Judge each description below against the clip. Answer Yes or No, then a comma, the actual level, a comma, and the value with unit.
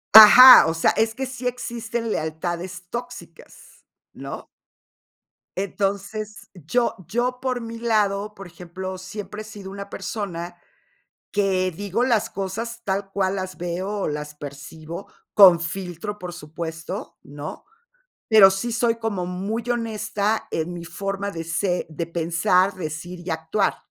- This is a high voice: Yes, high, 195 Hz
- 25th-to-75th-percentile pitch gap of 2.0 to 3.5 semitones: No, average, 4.0 semitones